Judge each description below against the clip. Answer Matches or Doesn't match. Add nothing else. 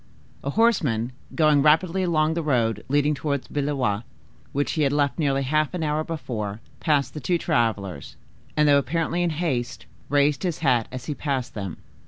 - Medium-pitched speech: Matches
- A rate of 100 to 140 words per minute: Doesn't match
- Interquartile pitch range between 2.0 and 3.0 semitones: Doesn't match